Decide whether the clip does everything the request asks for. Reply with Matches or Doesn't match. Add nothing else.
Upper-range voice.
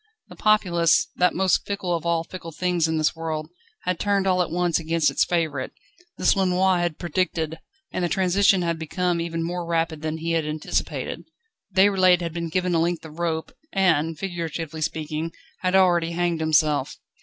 Doesn't match